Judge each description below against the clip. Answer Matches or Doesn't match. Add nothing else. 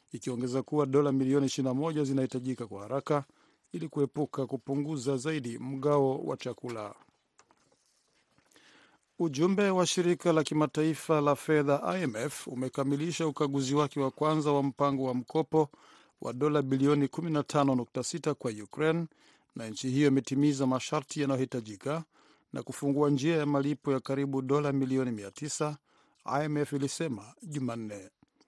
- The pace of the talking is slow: Doesn't match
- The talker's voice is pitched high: Doesn't match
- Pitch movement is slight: Matches